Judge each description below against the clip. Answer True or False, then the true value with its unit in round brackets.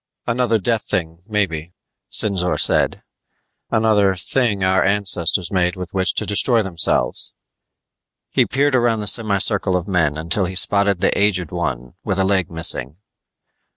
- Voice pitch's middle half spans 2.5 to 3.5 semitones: True (3.1 semitones)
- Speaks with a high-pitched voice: False (95 Hz)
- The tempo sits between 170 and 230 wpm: False (150 wpm)